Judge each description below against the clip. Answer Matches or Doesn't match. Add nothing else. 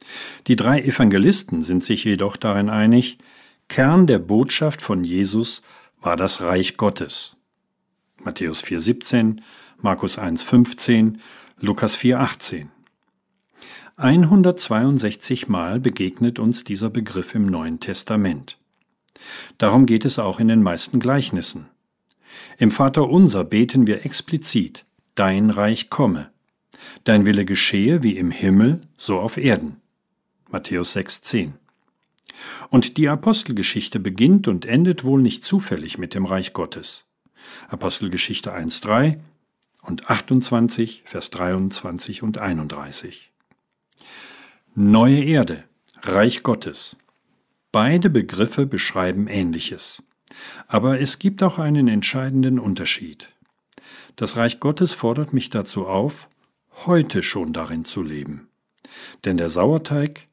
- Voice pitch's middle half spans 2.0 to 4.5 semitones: Doesn't match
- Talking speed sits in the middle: Doesn't match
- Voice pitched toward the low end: Matches